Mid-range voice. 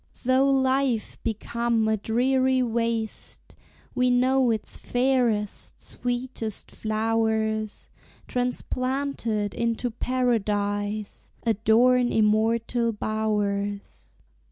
No: high, 230 Hz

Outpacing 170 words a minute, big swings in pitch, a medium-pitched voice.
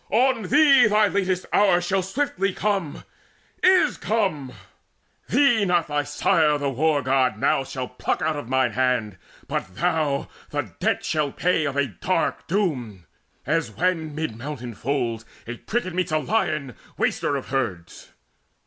No: average, 150 wpm; wide, 6.4 semitones; medium, 155 Hz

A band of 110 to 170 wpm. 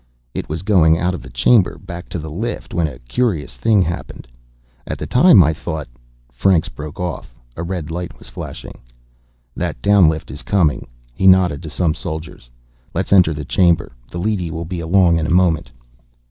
No: average, 190 wpm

